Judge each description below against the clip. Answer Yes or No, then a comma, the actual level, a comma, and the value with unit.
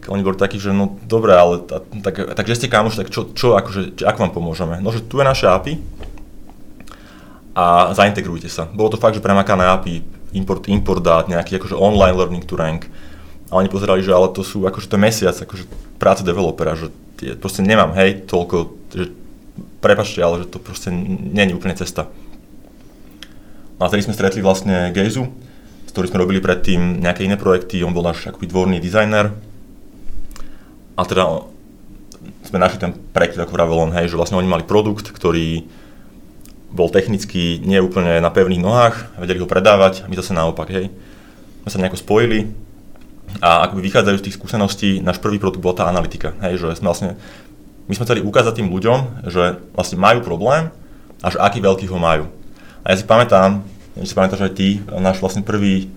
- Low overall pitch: Yes, very low, 95 Hz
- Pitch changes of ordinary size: No, narrow, 2.0 semitones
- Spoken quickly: Yes, fast, 185 wpm